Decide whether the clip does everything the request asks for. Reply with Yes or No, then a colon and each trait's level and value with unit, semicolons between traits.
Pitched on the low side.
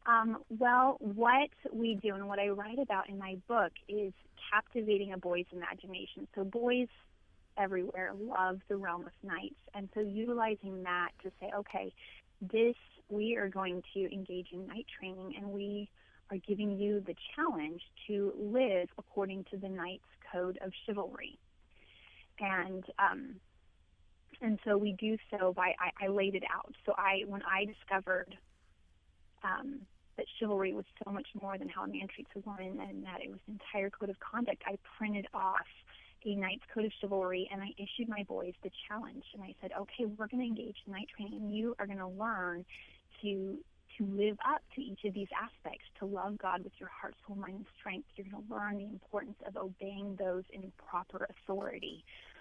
No: high, 200 Hz